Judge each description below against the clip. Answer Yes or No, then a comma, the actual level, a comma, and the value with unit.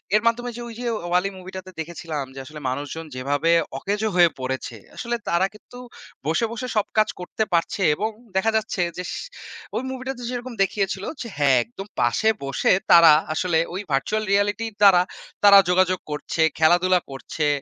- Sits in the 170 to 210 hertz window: Yes, medium, 185 Hz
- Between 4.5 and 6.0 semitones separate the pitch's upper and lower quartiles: Yes, average, 5.1 semitones